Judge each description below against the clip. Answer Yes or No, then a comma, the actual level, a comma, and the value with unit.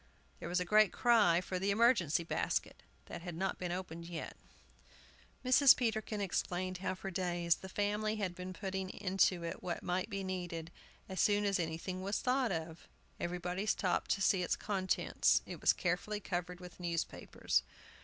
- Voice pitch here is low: No, medium, 185 Hz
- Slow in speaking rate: No, average, 170 wpm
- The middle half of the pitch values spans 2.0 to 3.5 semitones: Yes, narrow, 2.5 semitones